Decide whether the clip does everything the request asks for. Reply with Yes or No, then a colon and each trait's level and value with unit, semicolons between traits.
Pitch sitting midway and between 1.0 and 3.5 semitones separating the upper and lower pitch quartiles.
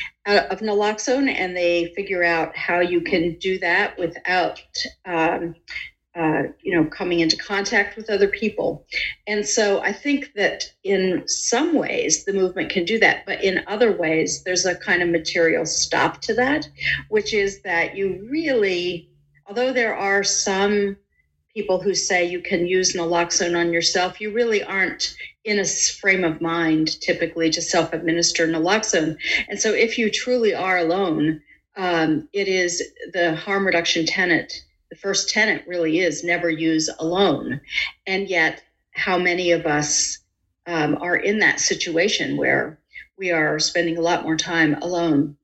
Yes: medium, 180 Hz; average, 3.2 semitones